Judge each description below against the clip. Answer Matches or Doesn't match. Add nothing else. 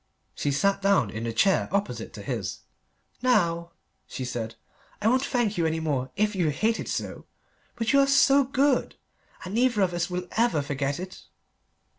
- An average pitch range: Doesn't match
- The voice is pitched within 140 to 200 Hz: Matches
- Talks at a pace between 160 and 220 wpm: Matches